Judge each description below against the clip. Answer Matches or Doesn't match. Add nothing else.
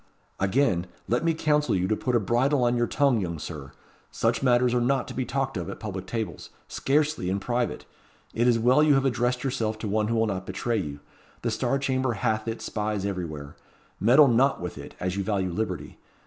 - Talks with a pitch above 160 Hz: Doesn't match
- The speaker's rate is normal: Doesn't match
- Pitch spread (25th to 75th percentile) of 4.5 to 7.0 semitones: Matches